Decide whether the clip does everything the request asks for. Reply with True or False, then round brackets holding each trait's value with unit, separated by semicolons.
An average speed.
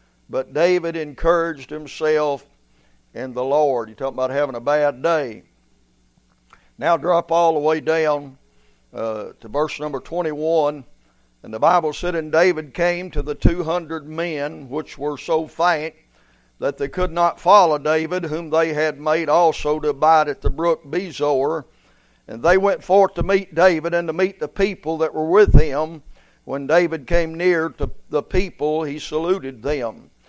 True (165 wpm)